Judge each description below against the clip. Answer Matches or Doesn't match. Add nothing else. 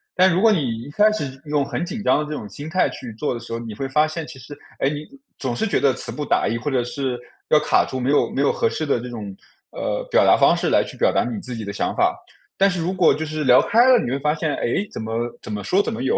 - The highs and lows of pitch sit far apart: Matches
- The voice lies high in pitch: Doesn't match